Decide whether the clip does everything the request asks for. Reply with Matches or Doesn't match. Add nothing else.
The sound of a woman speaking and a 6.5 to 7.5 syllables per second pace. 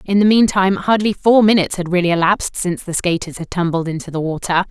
Matches